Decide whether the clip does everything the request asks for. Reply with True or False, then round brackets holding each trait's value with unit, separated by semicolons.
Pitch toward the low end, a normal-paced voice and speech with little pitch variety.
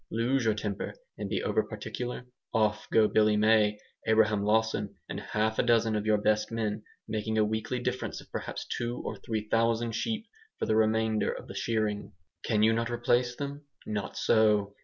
True (110 Hz; 180 wpm; 1.5 semitones)